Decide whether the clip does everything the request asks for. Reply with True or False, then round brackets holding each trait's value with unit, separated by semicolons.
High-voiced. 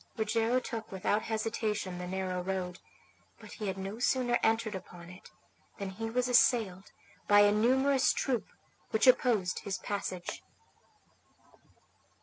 True (210 Hz)